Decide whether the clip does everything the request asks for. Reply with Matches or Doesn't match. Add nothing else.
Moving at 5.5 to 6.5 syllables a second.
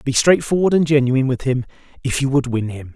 Matches